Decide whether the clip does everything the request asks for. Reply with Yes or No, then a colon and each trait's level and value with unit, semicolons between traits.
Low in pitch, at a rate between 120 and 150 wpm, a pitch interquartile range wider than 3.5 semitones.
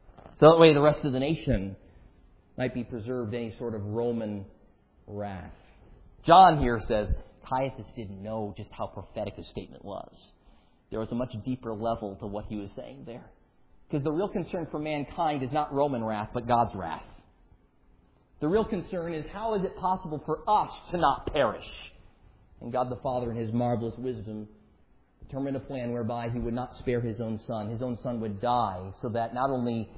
No: low, 120 Hz; average, 190 wpm; average, 4.1 semitones